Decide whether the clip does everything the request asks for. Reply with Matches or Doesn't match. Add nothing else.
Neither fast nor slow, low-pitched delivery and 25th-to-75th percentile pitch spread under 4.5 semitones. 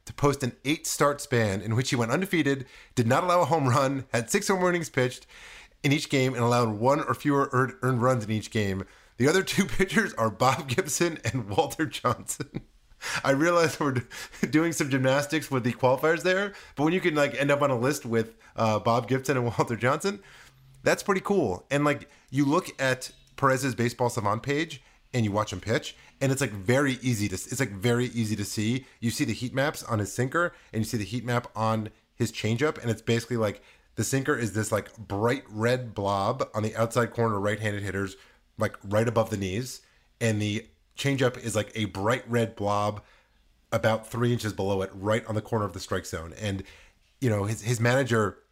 Doesn't match